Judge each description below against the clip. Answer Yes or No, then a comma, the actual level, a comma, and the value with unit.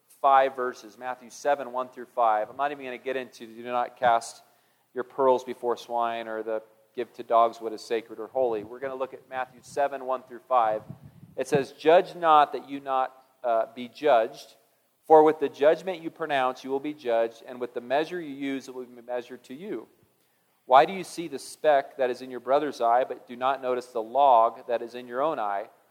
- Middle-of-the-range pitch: No, low, 125 Hz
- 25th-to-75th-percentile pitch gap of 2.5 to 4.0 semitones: Yes, average, 2.9 semitones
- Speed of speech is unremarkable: No, fast, 225 wpm